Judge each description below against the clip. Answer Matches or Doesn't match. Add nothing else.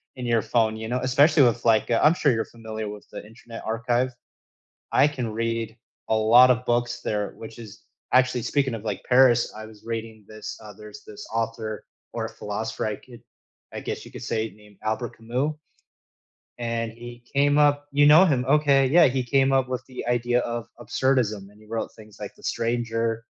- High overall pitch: Doesn't match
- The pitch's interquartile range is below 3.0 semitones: Matches